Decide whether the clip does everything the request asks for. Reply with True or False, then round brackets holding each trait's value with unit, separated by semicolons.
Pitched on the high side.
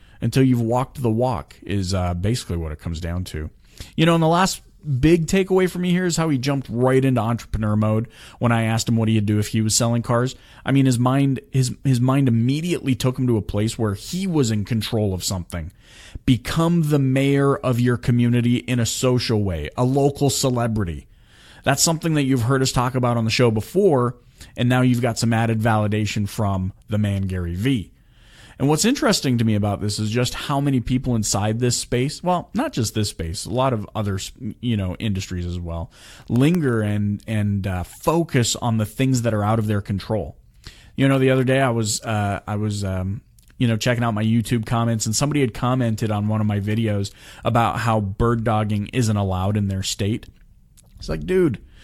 False (115 Hz)